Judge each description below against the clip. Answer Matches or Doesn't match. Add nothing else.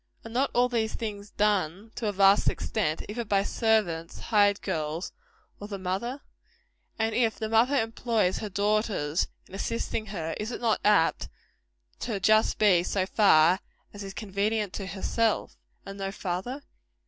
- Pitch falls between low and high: Doesn't match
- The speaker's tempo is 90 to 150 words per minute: Doesn't match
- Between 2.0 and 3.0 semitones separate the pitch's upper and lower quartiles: Matches